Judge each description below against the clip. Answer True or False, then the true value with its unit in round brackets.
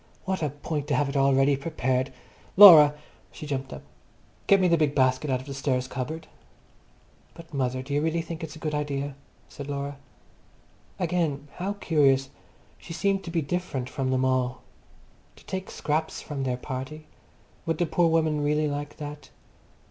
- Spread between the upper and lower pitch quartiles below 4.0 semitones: True (3.1 semitones)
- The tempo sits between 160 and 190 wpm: True (180 wpm)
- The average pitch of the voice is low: False (145 Hz)